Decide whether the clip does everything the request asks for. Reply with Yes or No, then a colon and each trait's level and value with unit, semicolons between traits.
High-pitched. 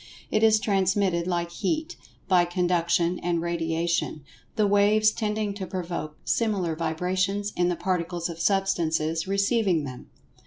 No: medium, 180 Hz